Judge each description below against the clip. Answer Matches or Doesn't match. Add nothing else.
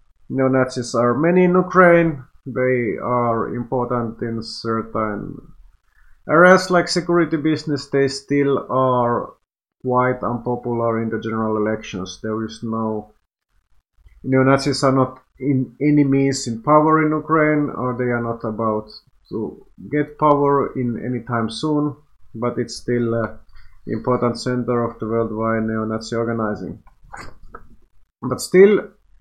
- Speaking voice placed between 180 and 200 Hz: Doesn't match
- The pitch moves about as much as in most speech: Matches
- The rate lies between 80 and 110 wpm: Doesn't match